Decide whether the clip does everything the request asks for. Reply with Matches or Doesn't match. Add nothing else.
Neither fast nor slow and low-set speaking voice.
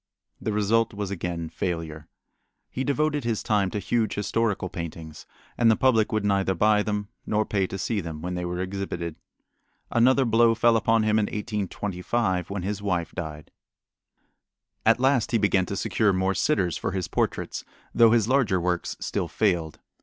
Matches